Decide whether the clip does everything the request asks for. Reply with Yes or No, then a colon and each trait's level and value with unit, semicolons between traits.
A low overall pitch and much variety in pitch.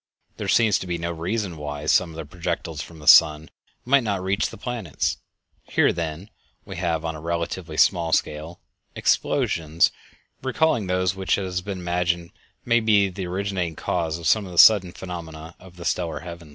No: very low, 85 Hz; average, 2.8 semitones